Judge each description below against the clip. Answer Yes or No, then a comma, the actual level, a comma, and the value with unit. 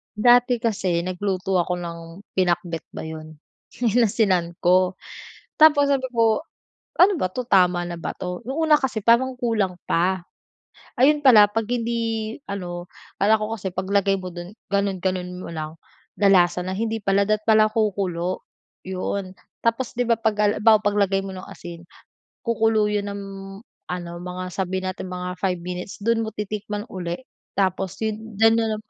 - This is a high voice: Yes, high, 200 Hz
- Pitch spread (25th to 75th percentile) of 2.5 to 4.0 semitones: Yes, average, 3.7 semitones